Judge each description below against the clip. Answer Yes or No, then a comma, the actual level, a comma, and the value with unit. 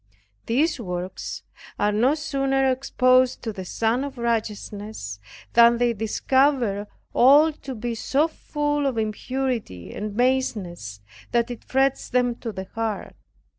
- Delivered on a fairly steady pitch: No, average, 4.1 semitones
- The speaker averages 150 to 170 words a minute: No, slow, 135 wpm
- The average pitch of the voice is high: Yes, high, 240 Hz